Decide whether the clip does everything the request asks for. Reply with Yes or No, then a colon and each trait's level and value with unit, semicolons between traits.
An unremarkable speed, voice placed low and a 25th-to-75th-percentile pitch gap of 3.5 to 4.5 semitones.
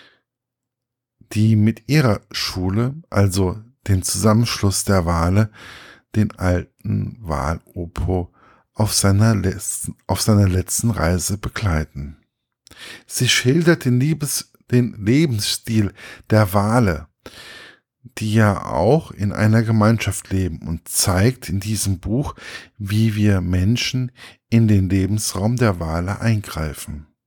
No: slow, 110 wpm; low, 105 Hz; average, 3.8 semitones